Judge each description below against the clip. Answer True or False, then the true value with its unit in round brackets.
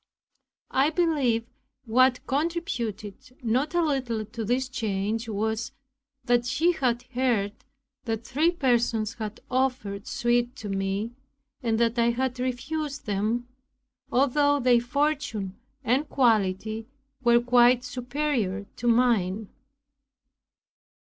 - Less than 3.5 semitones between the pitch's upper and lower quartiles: True (3.1 semitones)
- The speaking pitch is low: False (240 Hz)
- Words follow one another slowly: True (110 wpm)